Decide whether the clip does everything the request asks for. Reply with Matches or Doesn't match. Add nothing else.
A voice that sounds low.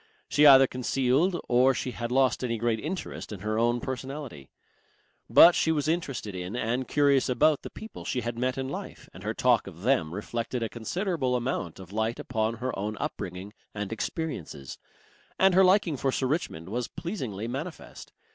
Matches